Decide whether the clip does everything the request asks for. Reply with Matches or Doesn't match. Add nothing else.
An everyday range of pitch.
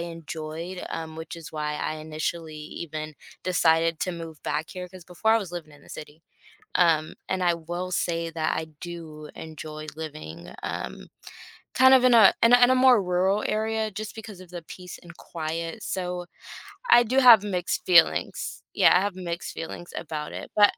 Matches